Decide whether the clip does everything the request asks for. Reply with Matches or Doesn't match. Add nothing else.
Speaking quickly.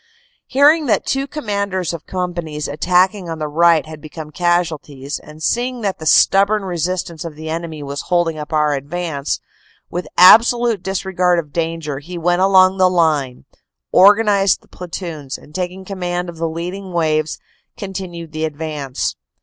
Doesn't match